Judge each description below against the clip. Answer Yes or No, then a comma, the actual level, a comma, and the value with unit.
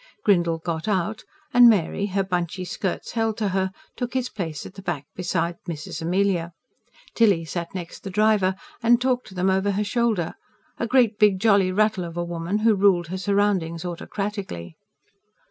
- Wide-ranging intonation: No, average, 3.5 semitones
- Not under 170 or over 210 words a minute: Yes, average, 175 wpm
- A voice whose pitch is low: No, high, 190 Hz